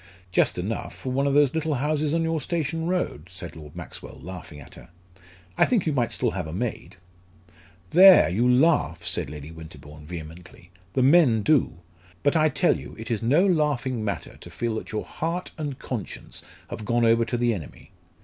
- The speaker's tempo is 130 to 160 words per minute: No, average, 190 wpm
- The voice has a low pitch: Yes, low, 120 Hz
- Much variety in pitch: Yes, wide, 8.9 semitones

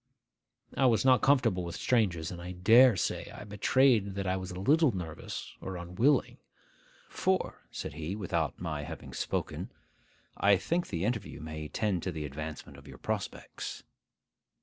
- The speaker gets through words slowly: No, average, 160 wpm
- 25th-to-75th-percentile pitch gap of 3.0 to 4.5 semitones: No, average, 5.2 semitones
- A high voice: No, very low, 95 Hz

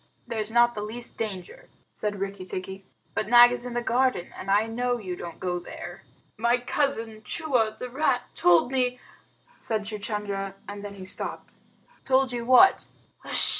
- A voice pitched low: No, high, 220 Hz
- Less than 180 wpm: Yes, average, 170 wpm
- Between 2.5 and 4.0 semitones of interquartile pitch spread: Yes, average, 3.7 semitones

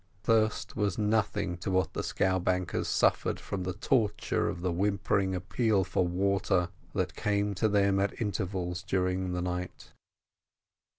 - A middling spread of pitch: No, narrow, 2.1 semitones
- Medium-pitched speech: No, very low, 95 Hz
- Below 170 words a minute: Yes, average, 140 wpm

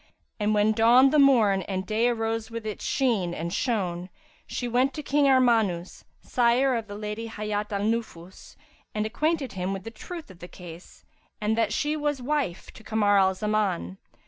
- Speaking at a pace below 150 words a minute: No, average, 180 wpm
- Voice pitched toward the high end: Yes, high, 220 Hz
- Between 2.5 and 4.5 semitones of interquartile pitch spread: Yes, average, 3.9 semitones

